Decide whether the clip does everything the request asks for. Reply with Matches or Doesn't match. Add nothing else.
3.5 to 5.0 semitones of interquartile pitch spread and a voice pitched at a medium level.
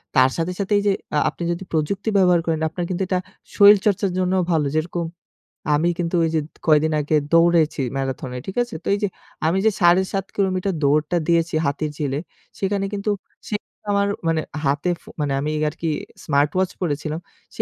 Matches